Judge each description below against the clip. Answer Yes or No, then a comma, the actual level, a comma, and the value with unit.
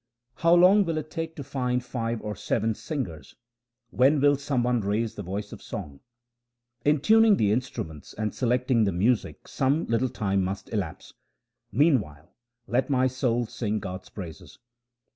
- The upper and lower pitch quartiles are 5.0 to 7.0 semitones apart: Yes, average, 5.3 semitones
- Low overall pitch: Yes, low, 120 Hz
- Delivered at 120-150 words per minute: No, average, 160 wpm